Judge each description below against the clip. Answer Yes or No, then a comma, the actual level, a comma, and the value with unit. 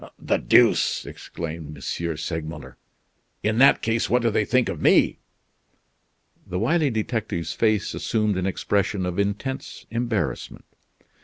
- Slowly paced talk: Yes, slow, 130 wpm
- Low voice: Yes, low, 105 Hz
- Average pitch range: Yes, average, 4.9 semitones